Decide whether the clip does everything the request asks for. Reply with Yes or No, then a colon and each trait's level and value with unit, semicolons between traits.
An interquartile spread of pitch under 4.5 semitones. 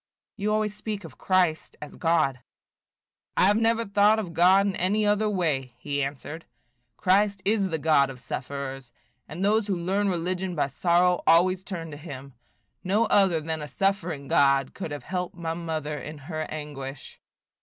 No: average, 5.0 semitones